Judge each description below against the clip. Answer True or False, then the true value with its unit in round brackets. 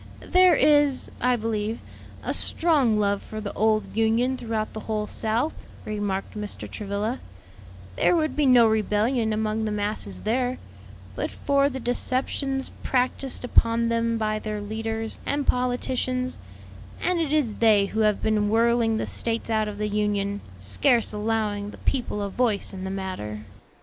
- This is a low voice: False (220 Hz)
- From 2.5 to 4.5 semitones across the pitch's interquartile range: True (3.1 semitones)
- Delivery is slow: False (155 wpm)